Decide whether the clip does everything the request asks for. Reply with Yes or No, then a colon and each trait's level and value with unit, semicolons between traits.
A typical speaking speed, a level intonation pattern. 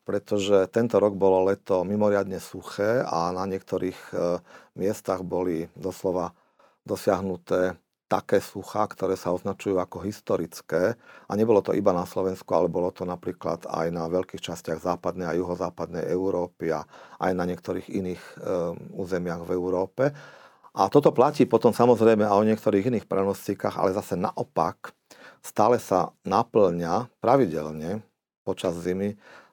Yes: average, 140 wpm; narrow, 1.8 semitones